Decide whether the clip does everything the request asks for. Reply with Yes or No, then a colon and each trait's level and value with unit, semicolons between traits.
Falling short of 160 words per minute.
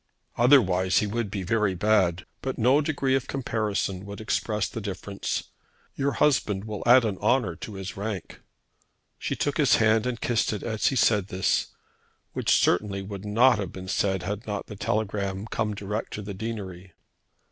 No: average, 175 wpm